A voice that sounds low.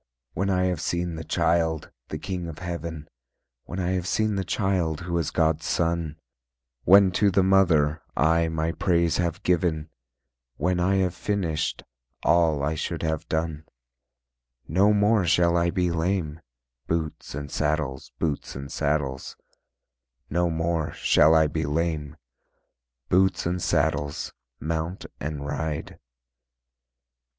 Yes: very low, 85 Hz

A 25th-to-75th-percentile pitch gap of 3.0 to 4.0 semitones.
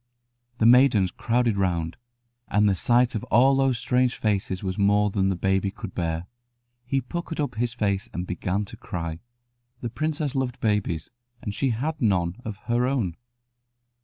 No: average, 4.6 semitones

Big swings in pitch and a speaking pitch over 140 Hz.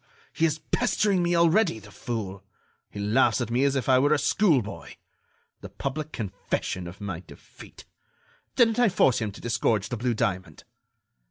No: wide, 7.6 semitones; low, 125 Hz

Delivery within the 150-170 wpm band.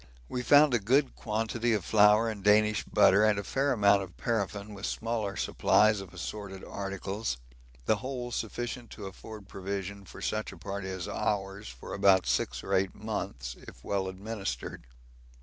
Yes: average, 165 wpm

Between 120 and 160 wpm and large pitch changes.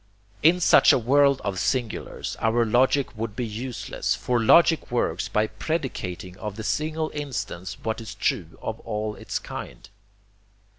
No: average, 150 wpm; average, 4.2 semitones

